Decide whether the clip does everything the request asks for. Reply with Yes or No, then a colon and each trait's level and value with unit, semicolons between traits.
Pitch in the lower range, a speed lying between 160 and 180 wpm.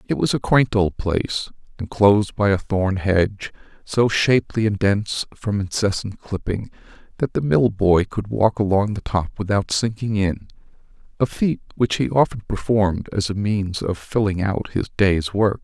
Yes: low, 100 Hz; average, 170 wpm